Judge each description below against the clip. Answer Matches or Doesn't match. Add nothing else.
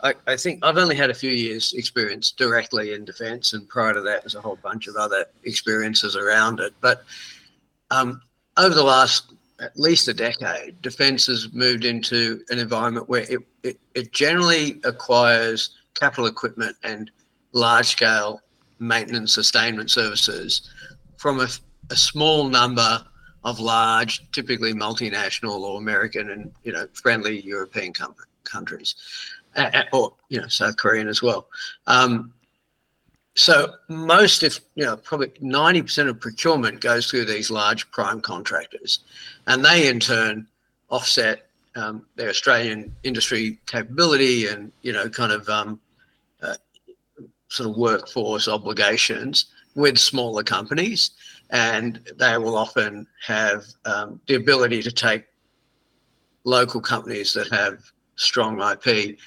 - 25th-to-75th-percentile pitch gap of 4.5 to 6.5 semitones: Doesn't match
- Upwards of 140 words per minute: Doesn't match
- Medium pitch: Doesn't match